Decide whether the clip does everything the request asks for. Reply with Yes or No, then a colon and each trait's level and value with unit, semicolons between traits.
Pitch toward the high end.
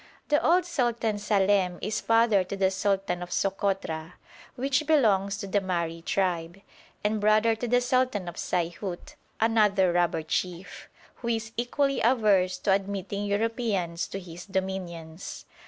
Yes: high, 200 Hz